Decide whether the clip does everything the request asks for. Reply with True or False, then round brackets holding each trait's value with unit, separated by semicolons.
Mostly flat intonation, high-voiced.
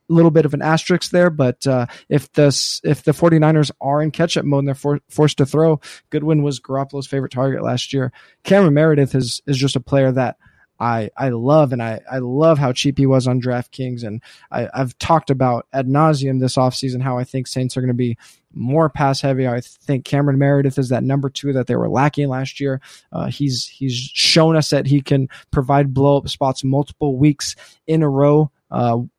False (2.3 semitones; 140 Hz)